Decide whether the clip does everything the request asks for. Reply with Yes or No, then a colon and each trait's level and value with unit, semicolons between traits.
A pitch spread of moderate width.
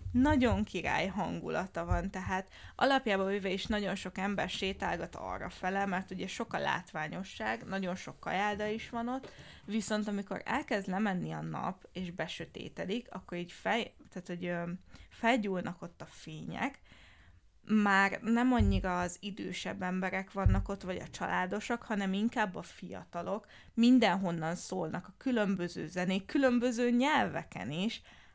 Yes: average, 3.1 semitones